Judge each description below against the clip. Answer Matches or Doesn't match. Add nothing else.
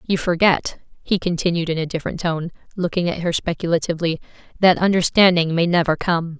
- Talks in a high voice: Doesn't match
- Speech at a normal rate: Matches